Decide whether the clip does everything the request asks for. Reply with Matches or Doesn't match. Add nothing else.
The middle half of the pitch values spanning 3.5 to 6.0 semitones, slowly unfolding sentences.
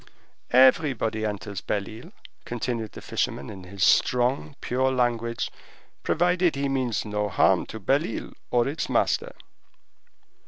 Matches